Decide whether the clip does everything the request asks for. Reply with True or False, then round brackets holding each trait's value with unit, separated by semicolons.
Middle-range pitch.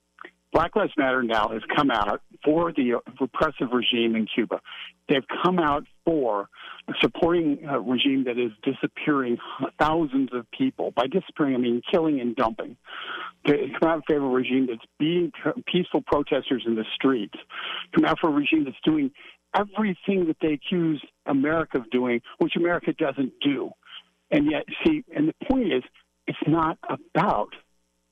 True (150 Hz)